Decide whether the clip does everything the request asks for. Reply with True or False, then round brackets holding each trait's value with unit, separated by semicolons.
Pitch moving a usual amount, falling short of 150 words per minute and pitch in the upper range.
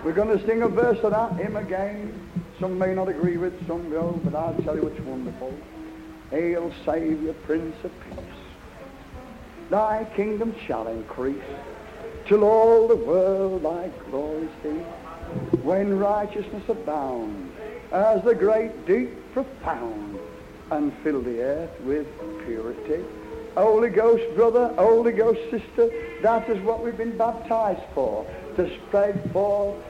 False (5.9 semitones; 135 wpm; 195 Hz)